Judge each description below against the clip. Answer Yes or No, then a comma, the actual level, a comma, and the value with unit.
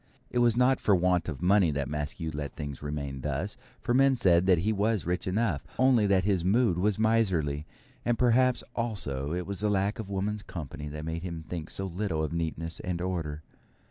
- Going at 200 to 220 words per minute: Yes, fast, 205 wpm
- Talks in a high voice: No, very low, 90 Hz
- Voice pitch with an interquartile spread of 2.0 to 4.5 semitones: No, average, 5.2 semitones